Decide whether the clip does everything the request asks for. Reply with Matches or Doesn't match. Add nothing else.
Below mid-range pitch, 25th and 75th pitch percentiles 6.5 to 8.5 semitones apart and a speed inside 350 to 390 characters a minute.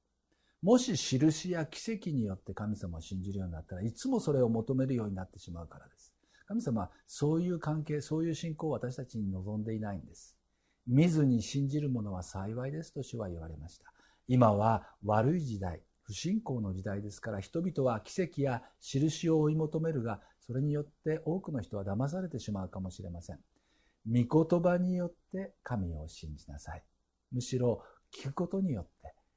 Matches